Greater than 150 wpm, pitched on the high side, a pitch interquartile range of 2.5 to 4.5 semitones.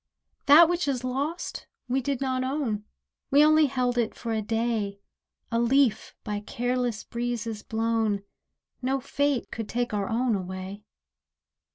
No: average, 145 wpm; high, 240 Hz; average, 3.4 semitones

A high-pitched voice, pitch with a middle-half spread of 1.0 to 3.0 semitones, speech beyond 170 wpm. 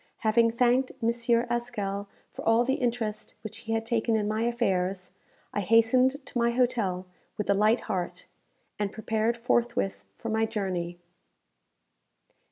No: high, 225 Hz; average, 2.7 semitones; average, 145 wpm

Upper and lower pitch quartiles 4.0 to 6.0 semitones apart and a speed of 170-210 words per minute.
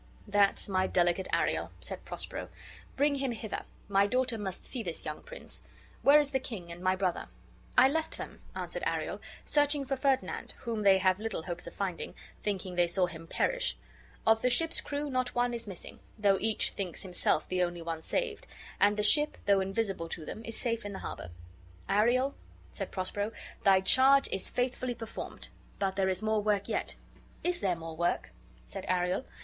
Yes: wide, 5.5 semitones; average, 190 wpm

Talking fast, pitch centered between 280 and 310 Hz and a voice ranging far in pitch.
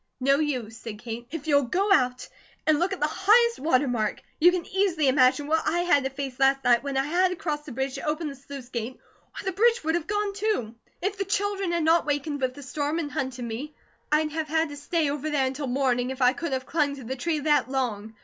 No: fast, 250 wpm; very high, 290 Hz; average, 4.4 semitones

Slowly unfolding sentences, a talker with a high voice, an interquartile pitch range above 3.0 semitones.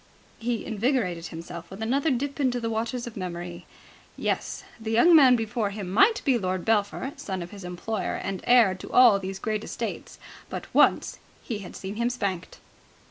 No: average, 180 wpm; high, 220 Hz; average, 4.6 semitones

